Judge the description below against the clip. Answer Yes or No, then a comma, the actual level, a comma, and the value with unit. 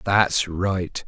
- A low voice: Yes, very low, 95 Hz